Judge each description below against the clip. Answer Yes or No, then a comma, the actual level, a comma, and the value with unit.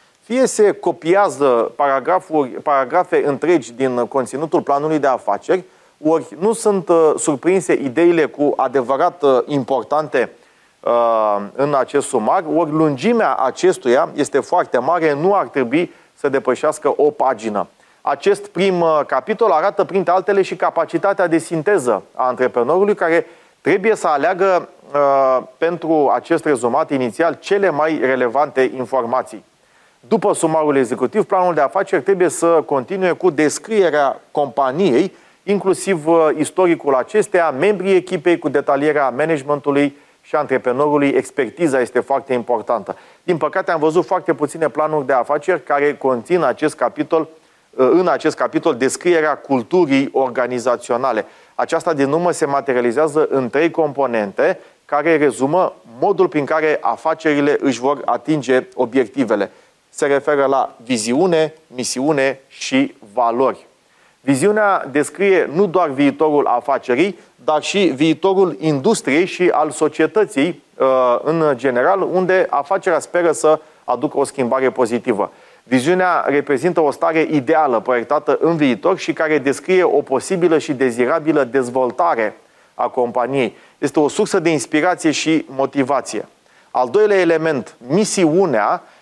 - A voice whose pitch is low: No, medium, 155 Hz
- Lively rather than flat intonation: No, average, 4.7 semitones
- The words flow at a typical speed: Yes, average, 125 wpm